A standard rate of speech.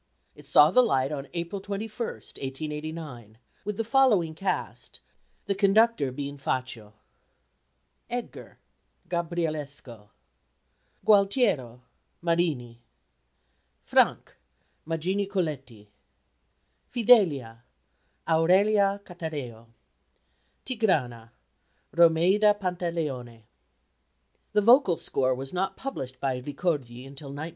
No: slow, 85 wpm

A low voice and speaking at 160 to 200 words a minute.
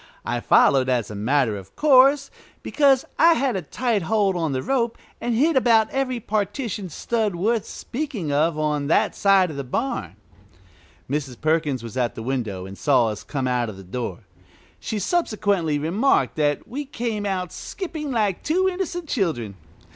No: high, 190 Hz; average, 170 wpm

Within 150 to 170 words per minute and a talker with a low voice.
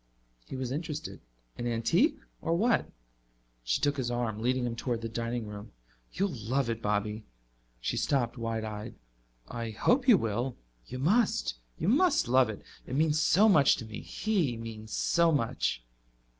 Yes: average, 165 wpm; low, 120 Hz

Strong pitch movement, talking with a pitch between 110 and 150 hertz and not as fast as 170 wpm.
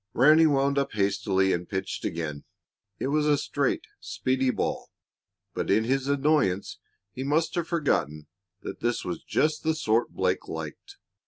Yes: wide, 7.2 semitones; low, 135 Hz; average, 155 wpm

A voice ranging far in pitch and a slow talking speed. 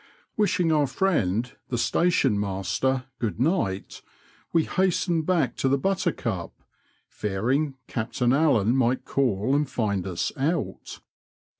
Yes: wide, 7.1 semitones; slow, 120 wpm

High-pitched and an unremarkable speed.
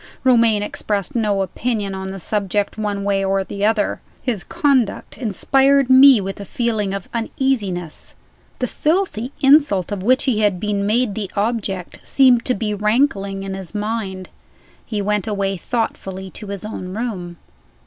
Yes: high, 210 Hz; average, 160 wpm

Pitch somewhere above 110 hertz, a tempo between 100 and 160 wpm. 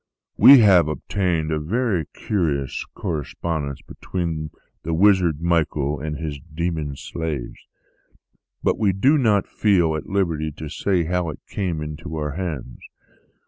No: very low, 80 Hz; slow, 135 wpm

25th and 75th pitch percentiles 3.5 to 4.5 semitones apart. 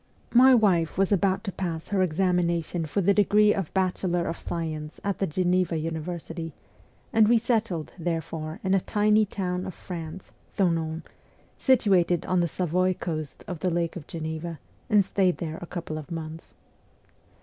No: average, 2.9 semitones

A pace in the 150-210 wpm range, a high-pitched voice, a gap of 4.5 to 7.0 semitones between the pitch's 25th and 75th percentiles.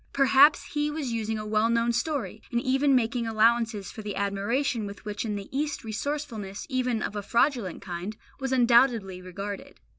No: average, 175 wpm; high, 230 Hz; average, 4.1 semitones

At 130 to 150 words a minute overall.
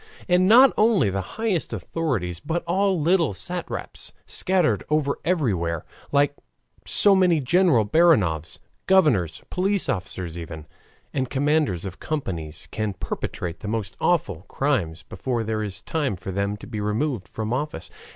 Yes: average, 140 wpm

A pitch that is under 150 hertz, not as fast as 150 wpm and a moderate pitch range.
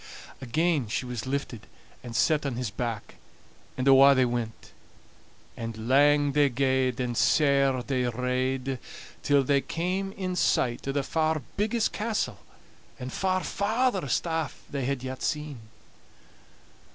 Yes: low, 135 Hz; average, 140 wpm; average, 3.8 semitones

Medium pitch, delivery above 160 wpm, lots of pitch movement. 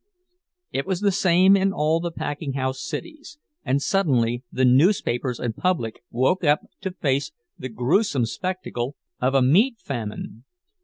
No: medium, 145 Hz; average, 150 wpm; wide, 6.7 semitones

